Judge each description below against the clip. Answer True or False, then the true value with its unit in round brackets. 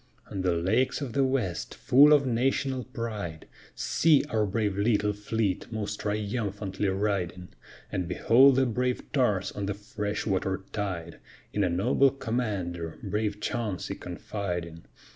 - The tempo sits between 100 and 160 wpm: True (140 wpm)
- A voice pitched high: False (105 Hz)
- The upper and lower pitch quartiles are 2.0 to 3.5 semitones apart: False (4.2 semitones)